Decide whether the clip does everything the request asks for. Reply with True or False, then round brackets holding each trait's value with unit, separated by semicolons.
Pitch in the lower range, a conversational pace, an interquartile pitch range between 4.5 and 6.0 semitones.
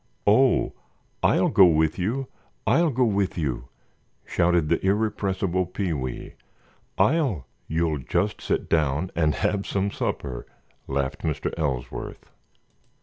False (90 Hz; 120 wpm; 4.9 semitones)